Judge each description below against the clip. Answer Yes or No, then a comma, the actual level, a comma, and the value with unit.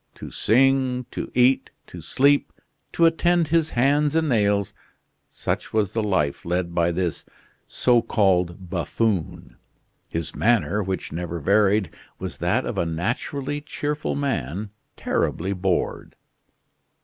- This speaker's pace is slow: Yes, slow, 130 wpm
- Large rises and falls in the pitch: Yes, wide, 7.2 semitones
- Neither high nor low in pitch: No, low, 105 Hz